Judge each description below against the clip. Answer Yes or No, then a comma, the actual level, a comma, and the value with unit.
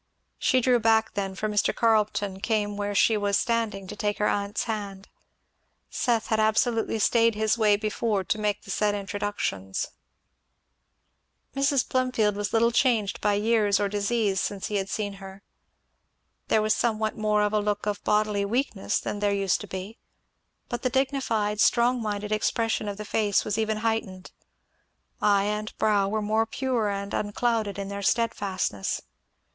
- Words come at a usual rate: Yes, average, 165 wpm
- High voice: Yes, high, 210 Hz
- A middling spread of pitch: No, narrow, 1.8 semitones